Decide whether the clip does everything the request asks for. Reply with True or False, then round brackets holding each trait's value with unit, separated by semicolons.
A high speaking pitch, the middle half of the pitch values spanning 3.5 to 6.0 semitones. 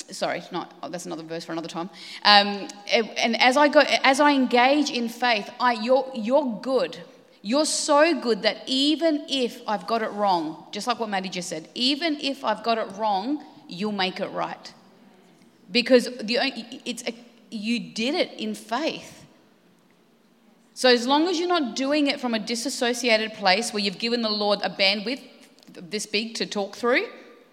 True (235 Hz; 4.3 semitones)